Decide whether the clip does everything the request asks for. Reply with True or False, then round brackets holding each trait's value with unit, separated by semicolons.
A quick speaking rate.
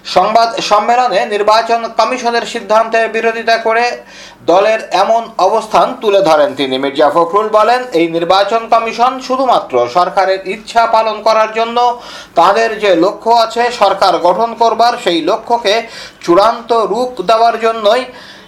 True (125 wpm)